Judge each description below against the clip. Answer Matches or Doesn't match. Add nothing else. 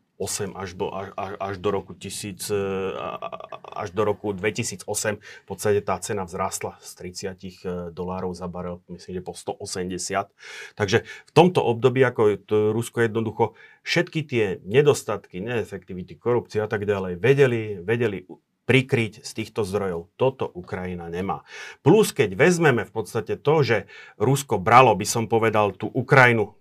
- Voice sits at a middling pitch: Doesn't match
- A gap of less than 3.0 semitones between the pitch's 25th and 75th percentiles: Doesn't match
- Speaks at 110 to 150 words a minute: Matches